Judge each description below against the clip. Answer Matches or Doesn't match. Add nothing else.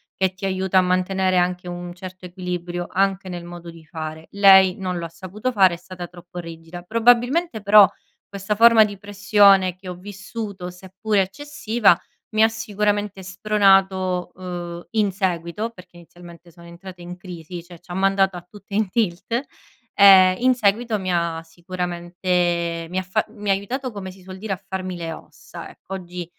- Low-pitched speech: Doesn't match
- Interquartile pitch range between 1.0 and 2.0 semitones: Doesn't match